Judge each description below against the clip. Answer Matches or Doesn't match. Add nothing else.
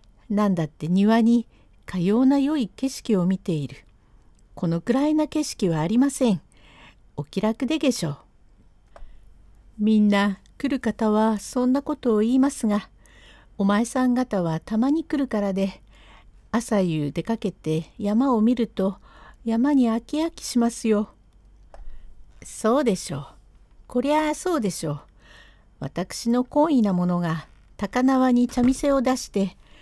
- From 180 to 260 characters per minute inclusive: Matches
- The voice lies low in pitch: Doesn't match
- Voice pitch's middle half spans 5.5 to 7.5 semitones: Matches